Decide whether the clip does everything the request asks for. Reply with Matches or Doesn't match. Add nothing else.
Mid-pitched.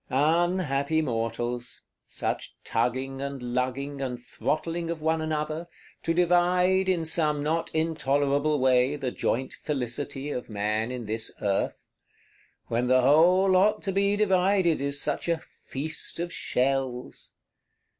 Matches